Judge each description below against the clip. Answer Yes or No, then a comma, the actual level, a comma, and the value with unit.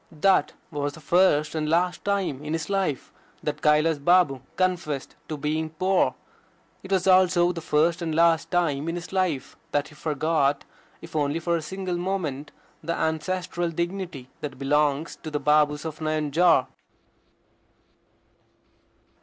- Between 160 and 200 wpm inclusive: No, average, 145 wpm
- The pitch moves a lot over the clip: No, average, 2.9 semitones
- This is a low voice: No, medium, 160 Hz